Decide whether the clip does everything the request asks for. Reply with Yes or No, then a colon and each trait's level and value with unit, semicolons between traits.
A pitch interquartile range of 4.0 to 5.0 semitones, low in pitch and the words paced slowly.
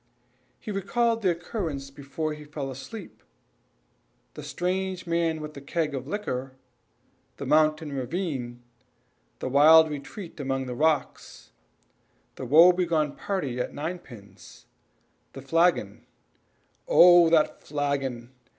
No: average, 4.4 semitones; medium, 155 Hz; slow, 115 wpm